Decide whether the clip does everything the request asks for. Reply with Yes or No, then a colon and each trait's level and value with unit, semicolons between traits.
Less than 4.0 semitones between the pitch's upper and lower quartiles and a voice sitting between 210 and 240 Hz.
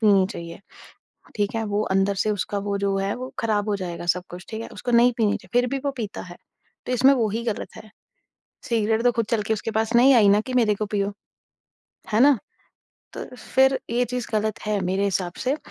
Yes: average, 2.9 semitones; high, 215 Hz